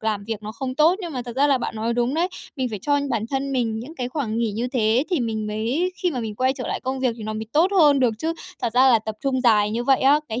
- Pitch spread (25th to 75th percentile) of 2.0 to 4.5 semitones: Yes, average, 3.7 semitones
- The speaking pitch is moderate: No, high, 245 Hz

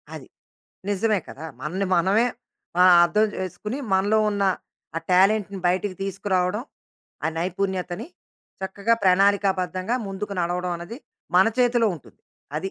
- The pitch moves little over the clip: Yes, narrow, 2.1 semitones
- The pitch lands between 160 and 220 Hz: Yes, high, 190 Hz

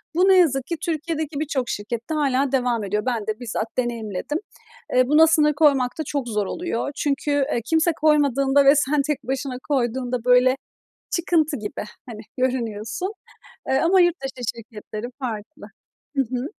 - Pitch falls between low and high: No, very high, 265 Hz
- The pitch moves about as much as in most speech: Yes, average, 4.0 semitones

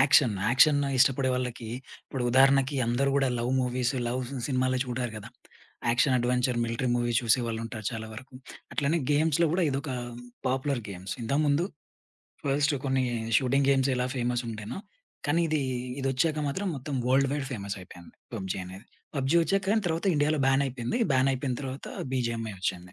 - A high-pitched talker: No, low, 130 Hz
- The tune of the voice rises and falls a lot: No, average, 2.9 semitones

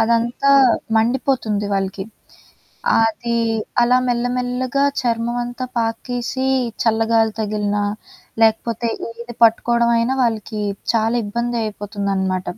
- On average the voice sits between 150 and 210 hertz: No, high, 230 Hz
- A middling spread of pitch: No, narrow, 2.1 semitones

